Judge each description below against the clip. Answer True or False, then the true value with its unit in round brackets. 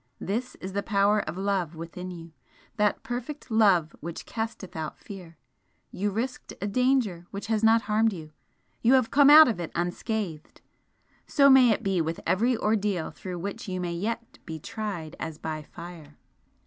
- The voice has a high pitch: True (200 Hz)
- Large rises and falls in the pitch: False (4.8 semitones)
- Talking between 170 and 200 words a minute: True (175 wpm)